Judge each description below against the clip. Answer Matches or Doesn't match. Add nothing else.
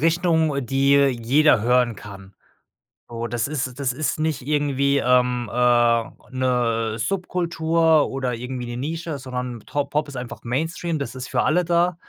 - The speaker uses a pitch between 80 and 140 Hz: Matches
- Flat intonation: Doesn't match